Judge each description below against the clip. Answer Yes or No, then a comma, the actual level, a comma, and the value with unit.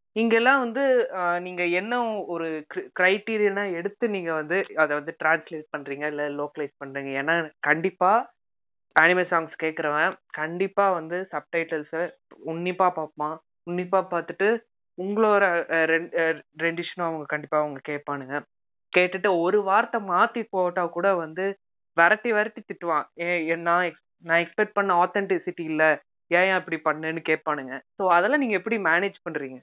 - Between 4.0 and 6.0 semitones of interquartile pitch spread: No, average, 3.5 semitones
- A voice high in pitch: No, medium, 170 Hz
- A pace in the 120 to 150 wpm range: Yes, average, 125 wpm